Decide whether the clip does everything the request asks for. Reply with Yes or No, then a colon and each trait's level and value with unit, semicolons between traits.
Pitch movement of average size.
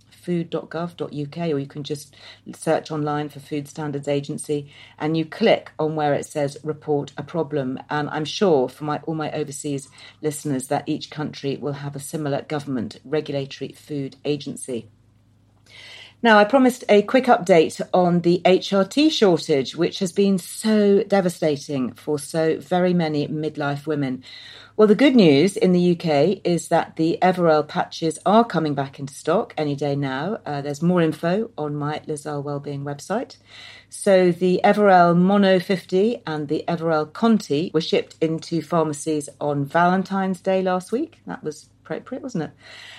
Yes: average, 3.8 semitones